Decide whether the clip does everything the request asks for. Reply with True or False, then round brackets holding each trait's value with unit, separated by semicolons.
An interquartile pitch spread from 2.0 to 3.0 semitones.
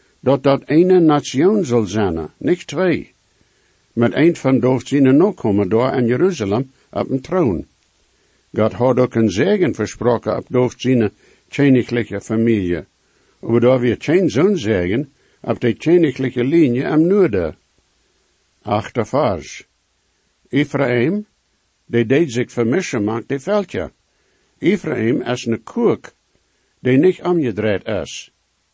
False (3.9 semitones)